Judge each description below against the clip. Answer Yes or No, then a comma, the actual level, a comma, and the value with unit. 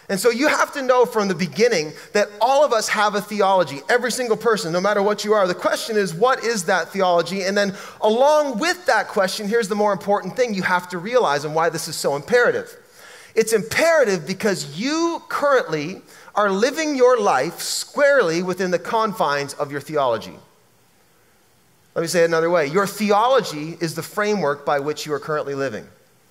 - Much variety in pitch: Yes, wide, 6.4 semitones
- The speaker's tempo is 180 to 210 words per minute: Yes, average, 195 wpm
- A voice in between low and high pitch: No, high, 205 Hz